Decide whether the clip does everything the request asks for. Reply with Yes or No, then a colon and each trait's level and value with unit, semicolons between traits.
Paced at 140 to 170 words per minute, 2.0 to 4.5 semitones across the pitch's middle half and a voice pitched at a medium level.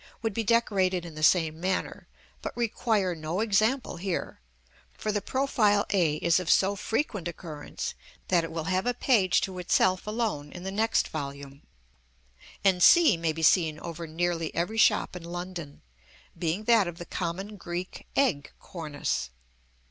Yes: average, 160 wpm; average, 4.1 semitones; medium, 180 Hz